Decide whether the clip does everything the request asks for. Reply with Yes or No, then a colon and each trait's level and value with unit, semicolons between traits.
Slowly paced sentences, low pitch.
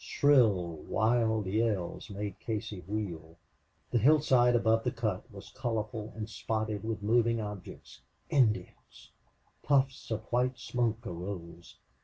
Yes: slow, 120 wpm; low, 110 Hz